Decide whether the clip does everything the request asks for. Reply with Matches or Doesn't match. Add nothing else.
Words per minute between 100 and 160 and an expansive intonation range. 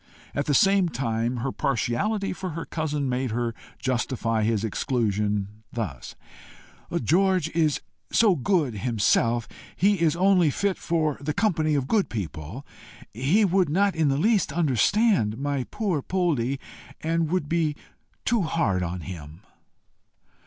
Matches